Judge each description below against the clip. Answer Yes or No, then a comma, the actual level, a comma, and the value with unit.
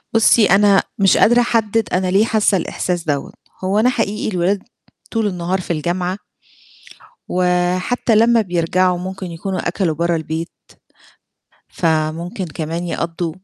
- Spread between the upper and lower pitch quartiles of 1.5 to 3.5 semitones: Yes, average, 3.2 semitones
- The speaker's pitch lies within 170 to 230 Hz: Yes, medium, 185 Hz